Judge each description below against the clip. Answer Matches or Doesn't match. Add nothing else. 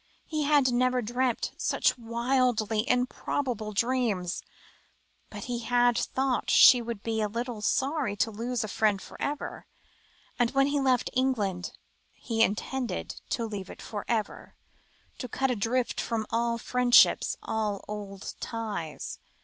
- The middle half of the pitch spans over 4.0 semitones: Doesn't match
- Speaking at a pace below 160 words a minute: Matches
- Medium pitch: Doesn't match